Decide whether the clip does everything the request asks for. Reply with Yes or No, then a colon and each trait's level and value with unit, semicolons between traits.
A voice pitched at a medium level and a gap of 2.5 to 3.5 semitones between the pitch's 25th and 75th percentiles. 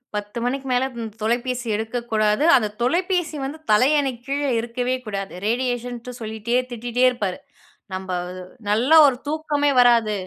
No: high, 245 Hz; average, 3.2 semitones